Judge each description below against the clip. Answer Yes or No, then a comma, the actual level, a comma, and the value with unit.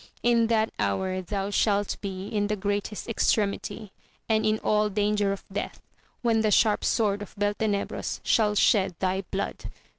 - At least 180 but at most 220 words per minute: No, average, 155 wpm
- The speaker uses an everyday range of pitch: No, narrow, 1.5 semitones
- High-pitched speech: Yes, high, 205 Hz